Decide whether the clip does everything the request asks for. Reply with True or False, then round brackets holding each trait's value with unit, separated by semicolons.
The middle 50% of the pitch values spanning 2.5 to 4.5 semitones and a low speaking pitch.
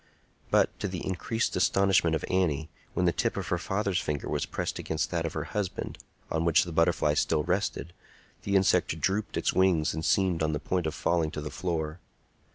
True (3.1 semitones; 85 Hz)